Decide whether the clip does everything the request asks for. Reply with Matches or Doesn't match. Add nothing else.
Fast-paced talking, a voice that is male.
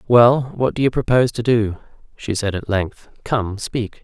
Doesn't match